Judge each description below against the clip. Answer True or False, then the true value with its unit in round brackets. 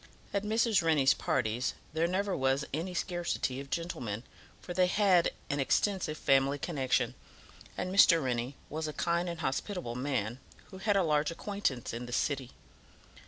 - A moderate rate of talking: True (160 wpm)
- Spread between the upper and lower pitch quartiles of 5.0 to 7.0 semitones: True (5.4 semitones)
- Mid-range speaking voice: True (155 Hz)